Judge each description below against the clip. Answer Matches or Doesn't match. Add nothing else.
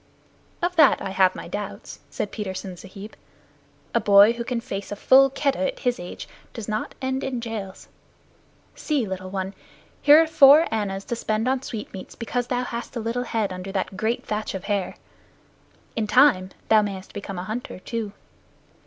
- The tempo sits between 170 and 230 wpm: Matches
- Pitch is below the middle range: Doesn't match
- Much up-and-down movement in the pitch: Doesn't match